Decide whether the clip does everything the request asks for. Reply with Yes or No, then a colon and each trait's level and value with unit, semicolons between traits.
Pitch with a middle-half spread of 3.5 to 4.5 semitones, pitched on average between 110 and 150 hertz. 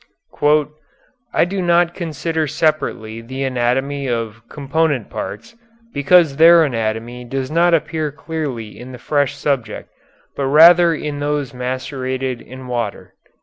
Yes: average, 4.2 semitones; medium, 140 Hz